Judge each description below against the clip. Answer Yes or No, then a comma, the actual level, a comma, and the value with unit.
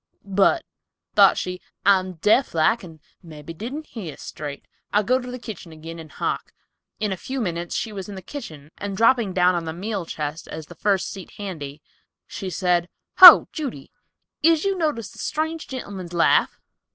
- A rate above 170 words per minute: Yes, average, 180 wpm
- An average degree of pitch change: No, wide, 5.8 semitones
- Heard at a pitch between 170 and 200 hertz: Yes, high, 190 Hz